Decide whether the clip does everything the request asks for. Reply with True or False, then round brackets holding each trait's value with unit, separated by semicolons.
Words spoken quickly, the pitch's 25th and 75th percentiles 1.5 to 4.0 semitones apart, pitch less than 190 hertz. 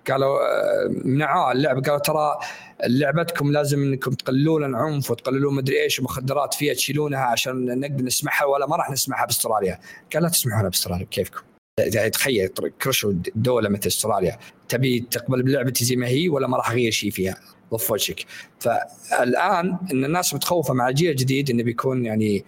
True (155 wpm; 2.6 semitones; 135 Hz)